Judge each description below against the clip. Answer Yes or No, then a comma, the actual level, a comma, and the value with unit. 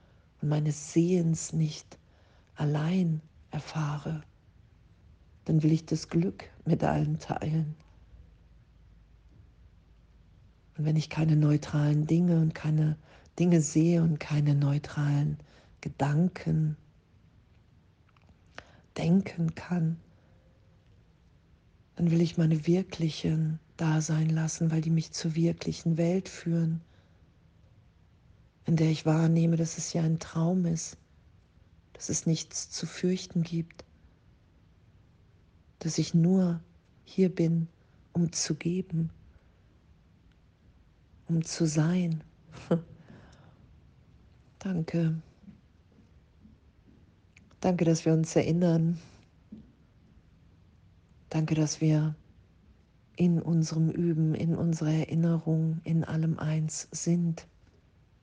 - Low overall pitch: No, medium, 155 Hz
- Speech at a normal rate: No, slow, 95 wpm